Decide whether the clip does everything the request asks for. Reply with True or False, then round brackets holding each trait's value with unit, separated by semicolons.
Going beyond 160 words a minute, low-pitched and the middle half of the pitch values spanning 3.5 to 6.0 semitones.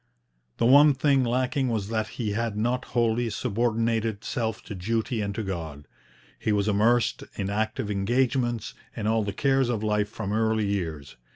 False (170 wpm; 110 Hz; 2.7 semitones)